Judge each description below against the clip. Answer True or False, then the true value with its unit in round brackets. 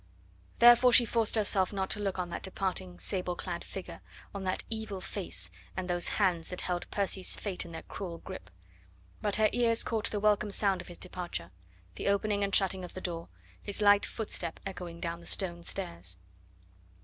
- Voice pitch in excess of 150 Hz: True (190 Hz)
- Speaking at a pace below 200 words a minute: True (185 wpm)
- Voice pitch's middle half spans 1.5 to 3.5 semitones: True (2.8 semitones)